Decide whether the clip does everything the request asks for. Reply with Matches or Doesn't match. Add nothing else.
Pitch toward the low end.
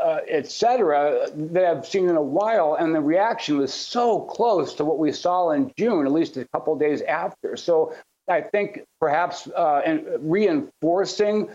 Doesn't match